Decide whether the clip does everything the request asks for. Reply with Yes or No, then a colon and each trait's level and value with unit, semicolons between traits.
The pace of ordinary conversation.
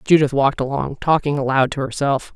Yes: average, 180 wpm